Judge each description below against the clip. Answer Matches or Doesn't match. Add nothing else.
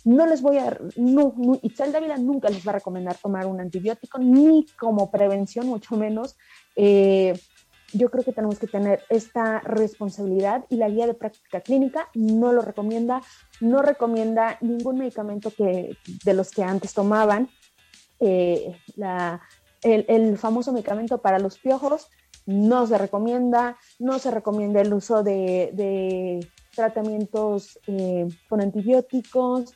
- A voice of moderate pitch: Doesn't match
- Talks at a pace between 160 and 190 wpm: Doesn't match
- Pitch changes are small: Doesn't match